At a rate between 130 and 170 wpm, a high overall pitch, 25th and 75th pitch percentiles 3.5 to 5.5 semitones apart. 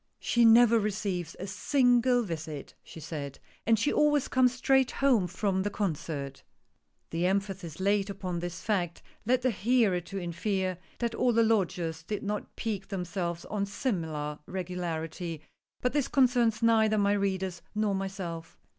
Yes: average, 155 wpm; high, 195 Hz; average, 4.7 semitones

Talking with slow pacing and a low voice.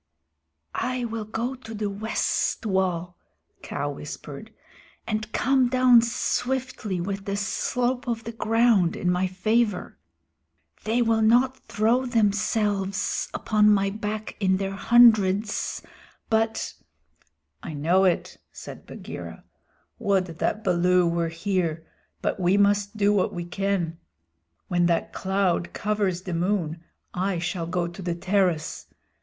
No: slow, 130 wpm; high, 200 Hz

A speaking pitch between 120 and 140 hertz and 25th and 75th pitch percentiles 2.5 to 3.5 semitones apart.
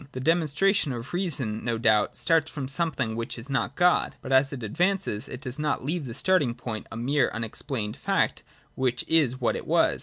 No: low, 135 Hz; average, 5.3 semitones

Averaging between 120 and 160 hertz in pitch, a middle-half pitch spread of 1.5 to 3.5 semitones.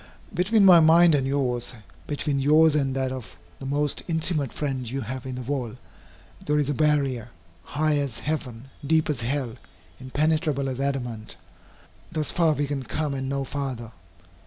Yes: medium, 140 Hz; average, 2.8 semitones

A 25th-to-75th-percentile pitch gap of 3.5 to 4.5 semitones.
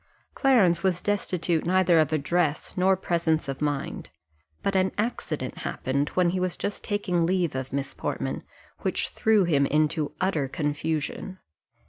Yes: average, 4.0 semitones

